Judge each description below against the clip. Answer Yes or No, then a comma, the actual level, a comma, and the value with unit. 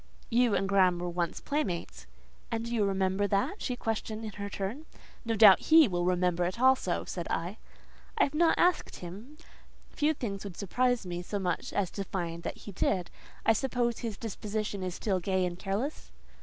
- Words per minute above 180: Yes, average, 190 wpm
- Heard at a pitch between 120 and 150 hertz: No, high, 200 Hz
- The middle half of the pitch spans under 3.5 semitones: No, average, 4.4 semitones